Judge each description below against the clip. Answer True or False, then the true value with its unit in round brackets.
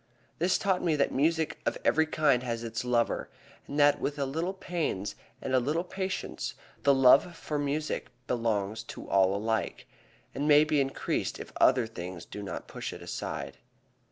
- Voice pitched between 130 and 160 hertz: True (140 Hz)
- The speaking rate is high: False (175 wpm)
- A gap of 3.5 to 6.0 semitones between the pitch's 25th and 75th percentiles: True (5.3 semitones)